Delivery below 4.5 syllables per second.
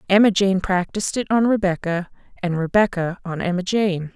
No: 5.3 syllables/s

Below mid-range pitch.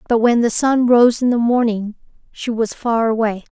No: high, 230 Hz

